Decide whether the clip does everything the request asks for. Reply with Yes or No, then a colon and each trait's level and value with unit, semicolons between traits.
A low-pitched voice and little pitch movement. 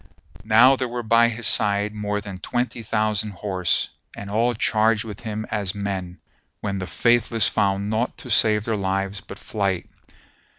Yes: low, 105 Hz; narrow, 2.3 semitones